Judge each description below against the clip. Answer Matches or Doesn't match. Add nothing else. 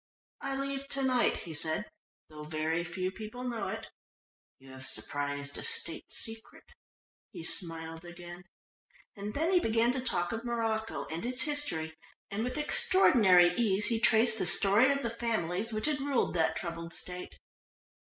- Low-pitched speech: Doesn't match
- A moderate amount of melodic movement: Doesn't match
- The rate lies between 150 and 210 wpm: Matches